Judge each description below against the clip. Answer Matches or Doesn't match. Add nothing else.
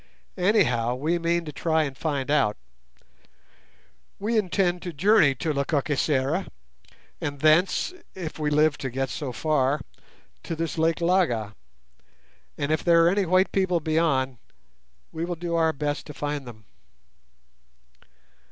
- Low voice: Doesn't match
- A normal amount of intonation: Matches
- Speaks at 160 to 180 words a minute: Doesn't match